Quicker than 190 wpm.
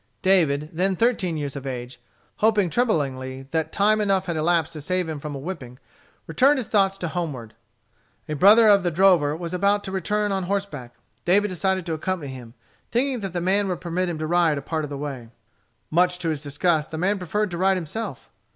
Yes: fast, 205 wpm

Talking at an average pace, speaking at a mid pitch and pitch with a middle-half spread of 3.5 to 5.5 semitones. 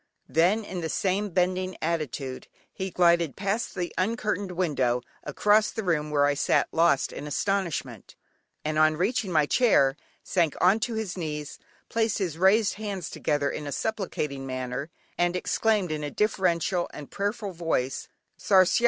Yes: average, 155 wpm; medium, 175 Hz; average, 4.9 semitones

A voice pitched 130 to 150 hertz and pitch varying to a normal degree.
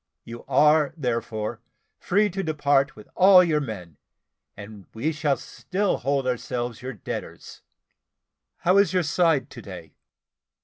No: medium, 140 Hz; wide, 5.7 semitones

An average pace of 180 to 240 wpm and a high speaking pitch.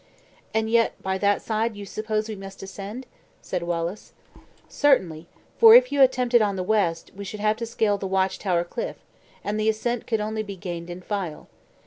Yes: average, 195 wpm; high, 210 Hz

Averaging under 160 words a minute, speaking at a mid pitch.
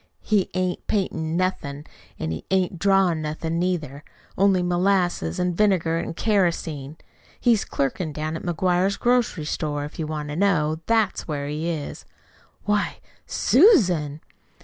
Yes: average, 140 wpm; medium, 170 Hz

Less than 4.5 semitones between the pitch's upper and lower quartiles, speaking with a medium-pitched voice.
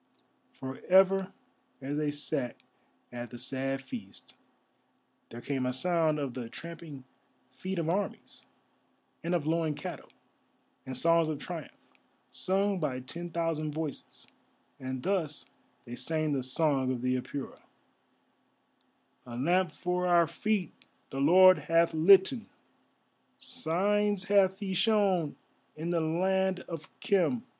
No: average, 5.3 semitones; medium, 165 Hz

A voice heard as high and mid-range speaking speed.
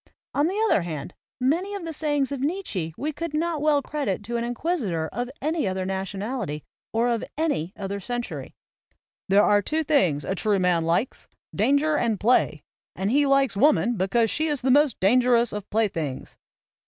Yes: high, 240 Hz; average, 185 wpm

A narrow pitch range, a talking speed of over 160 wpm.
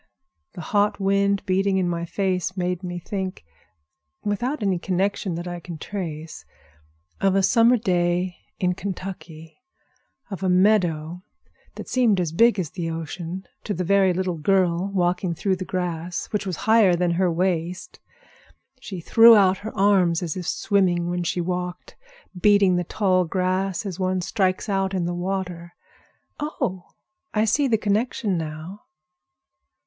No: narrow, 2.2 semitones; average, 150 wpm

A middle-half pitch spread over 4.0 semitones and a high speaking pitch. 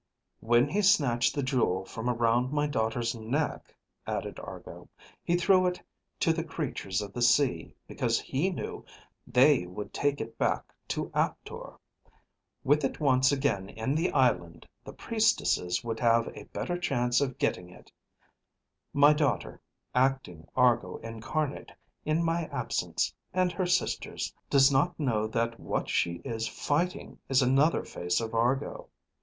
No: average, 4.5 semitones; low, 130 Hz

